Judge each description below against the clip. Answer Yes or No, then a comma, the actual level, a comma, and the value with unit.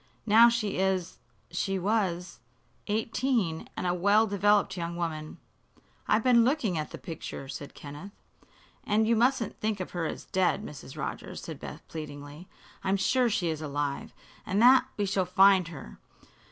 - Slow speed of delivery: No, average, 160 wpm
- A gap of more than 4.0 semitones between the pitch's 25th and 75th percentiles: Yes, average, 4.5 semitones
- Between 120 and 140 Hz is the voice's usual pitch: No, high, 190 Hz